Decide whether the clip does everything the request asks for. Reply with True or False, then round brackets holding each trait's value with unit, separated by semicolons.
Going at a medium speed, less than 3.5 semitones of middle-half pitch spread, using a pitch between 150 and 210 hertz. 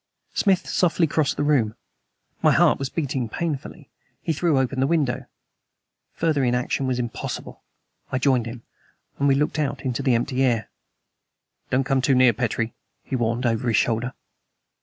False (160 wpm; 3.1 semitones; 130 Hz)